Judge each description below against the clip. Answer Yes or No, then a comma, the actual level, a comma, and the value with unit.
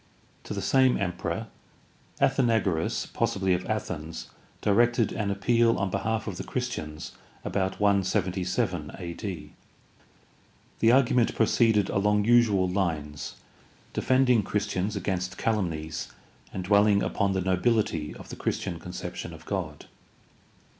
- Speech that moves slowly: Yes, slow, 120 wpm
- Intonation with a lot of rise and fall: No, average, 3.9 semitones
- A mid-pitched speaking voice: No, low, 100 Hz